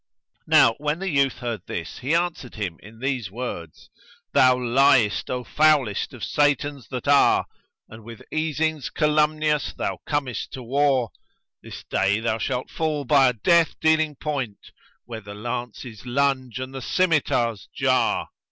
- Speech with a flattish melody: No, average, 4.3 semitones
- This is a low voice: Yes, low, 130 Hz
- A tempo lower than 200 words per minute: Yes, average, 155 wpm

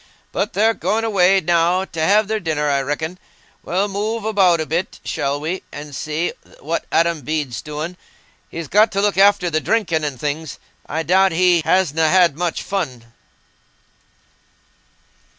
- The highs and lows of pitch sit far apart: No, average, 4.0 semitones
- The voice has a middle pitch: Yes, medium, 170 Hz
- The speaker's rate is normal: Yes, average, 155 wpm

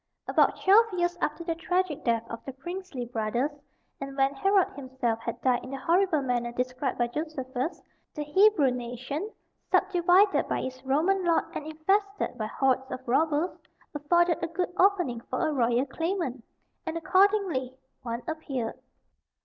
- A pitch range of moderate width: No, wide, 5.7 semitones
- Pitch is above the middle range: Yes, very high, 290 Hz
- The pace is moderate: Yes, average, 155 wpm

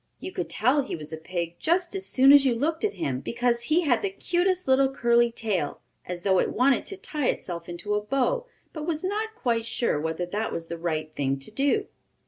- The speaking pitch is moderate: No, high, 240 Hz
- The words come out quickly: Yes, fast, 225 wpm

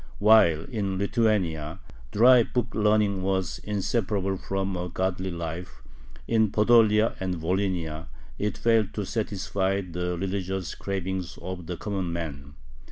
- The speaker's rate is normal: No, slow, 125 wpm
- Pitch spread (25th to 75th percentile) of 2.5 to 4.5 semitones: Yes, average, 2.9 semitones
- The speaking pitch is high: No, very low, 95 Hz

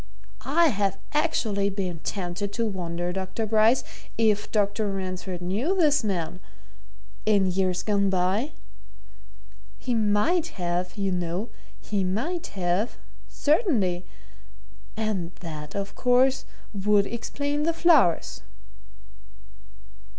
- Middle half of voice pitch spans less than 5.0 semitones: Yes, average, 4.2 semitones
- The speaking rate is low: Yes, slow, 105 wpm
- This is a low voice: No, high, 200 Hz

